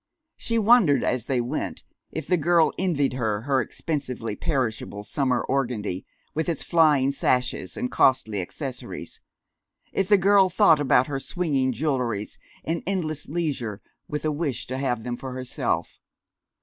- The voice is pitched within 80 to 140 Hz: Yes, low, 135 Hz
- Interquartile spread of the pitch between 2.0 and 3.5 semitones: No, average, 4.6 semitones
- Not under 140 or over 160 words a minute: Yes, average, 150 wpm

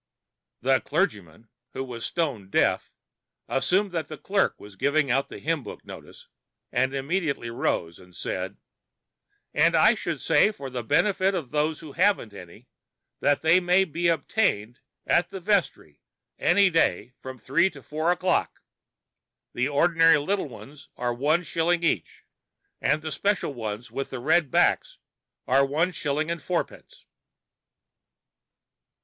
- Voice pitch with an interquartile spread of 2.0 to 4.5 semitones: No, average, 5.2 semitones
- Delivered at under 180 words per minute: Yes, average, 145 wpm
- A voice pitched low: No, medium, 150 Hz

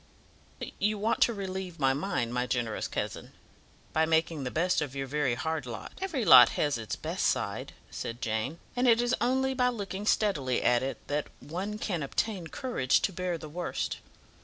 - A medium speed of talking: Yes, average, 185 wpm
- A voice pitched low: No, medium, 165 Hz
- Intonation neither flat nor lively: No, wide, 7.7 semitones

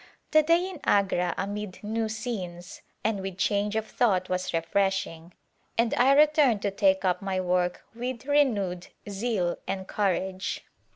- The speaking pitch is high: Yes, high, 200 Hz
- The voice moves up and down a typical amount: Yes, average, 3.9 semitones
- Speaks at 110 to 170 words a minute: Yes, average, 150 wpm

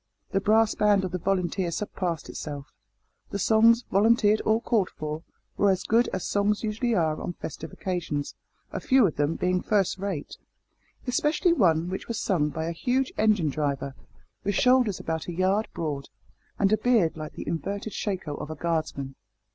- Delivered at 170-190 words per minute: Yes, average, 175 wpm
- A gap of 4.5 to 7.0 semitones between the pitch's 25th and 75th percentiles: Yes, average, 5.1 semitones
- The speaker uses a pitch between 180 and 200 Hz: Yes, high, 190 Hz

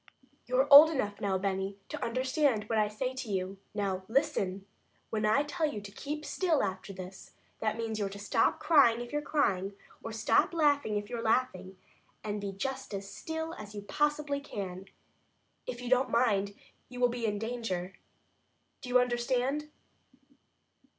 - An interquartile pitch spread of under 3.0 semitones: No, average, 5.0 semitones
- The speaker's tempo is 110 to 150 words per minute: No, average, 170 wpm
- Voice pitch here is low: No, high, 225 Hz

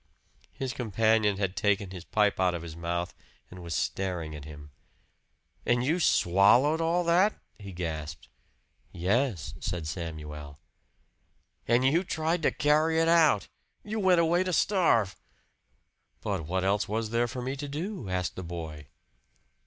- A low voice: Yes, low, 105 Hz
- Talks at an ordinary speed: Yes, average, 150 wpm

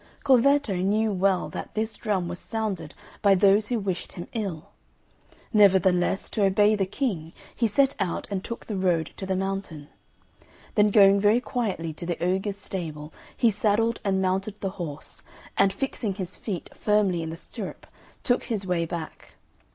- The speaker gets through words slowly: No, average, 165 wpm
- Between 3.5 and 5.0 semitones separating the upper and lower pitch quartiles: No, average, 3.0 semitones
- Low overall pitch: No, high, 195 Hz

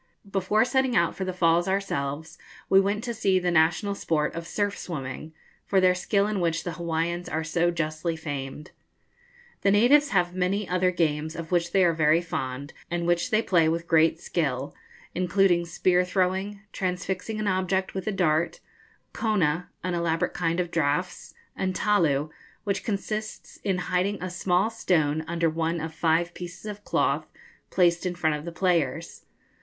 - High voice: No, medium, 175 Hz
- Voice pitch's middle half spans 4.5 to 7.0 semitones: No, average, 2.8 semitones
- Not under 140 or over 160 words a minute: No, average, 170 wpm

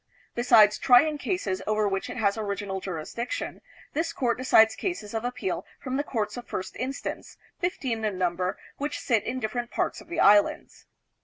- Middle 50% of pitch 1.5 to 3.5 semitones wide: No, average, 4.2 semitones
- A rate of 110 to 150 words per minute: No, average, 175 wpm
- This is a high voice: Yes, high, 225 Hz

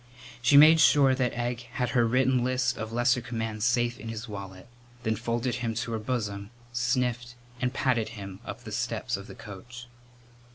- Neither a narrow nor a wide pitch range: No, narrow, 2.0 semitones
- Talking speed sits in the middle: Yes, average, 180 wpm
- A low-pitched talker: Yes, low, 120 Hz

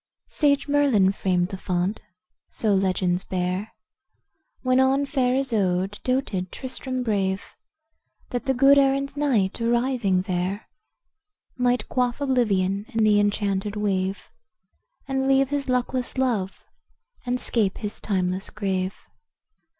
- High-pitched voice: Yes, high, 220 Hz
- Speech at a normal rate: No, slow, 120 wpm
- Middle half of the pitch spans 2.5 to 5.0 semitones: No, wide, 5.5 semitones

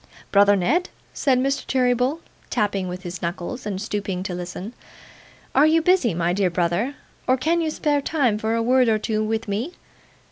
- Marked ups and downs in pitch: Yes, wide, 5.8 semitones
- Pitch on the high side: Yes, high, 220 Hz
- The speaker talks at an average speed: Yes, average, 180 wpm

